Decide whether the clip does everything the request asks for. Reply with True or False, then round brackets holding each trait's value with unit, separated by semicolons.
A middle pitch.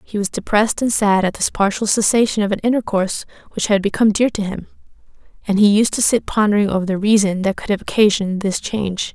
False (205 Hz)